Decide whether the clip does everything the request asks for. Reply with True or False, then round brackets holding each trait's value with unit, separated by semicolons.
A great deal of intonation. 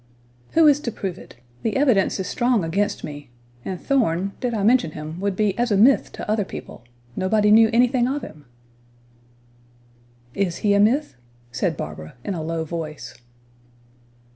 True (6.3 semitones)